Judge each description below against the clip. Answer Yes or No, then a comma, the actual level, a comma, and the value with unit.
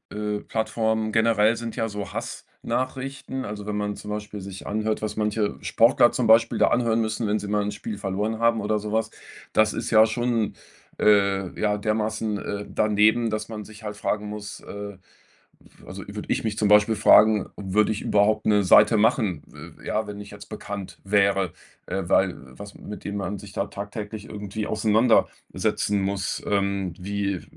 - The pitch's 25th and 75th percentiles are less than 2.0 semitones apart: Yes, narrow, 1.3 semitones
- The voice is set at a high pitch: No, low, 105 Hz